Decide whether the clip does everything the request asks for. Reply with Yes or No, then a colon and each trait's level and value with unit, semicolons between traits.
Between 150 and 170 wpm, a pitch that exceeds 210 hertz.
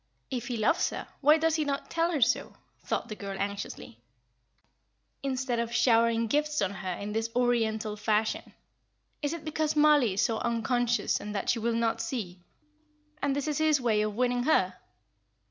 No: average, 180 wpm; high, 235 Hz